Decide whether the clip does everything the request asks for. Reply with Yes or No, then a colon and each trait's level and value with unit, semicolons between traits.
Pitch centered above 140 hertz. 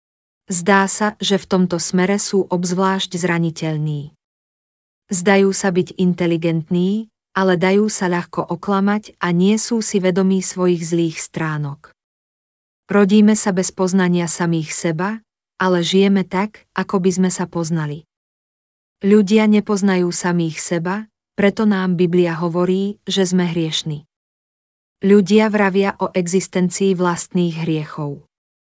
Yes: medium, 185 Hz